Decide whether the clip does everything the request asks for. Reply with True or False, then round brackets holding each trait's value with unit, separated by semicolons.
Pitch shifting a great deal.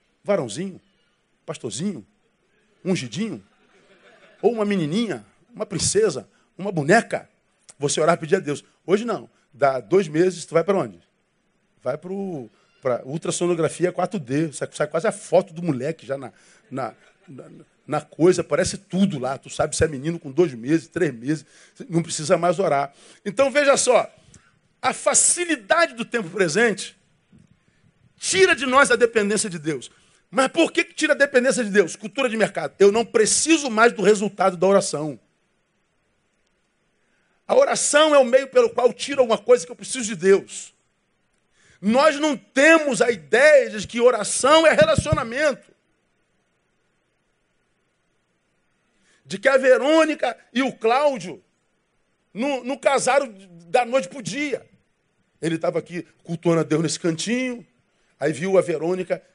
True (7.2 semitones)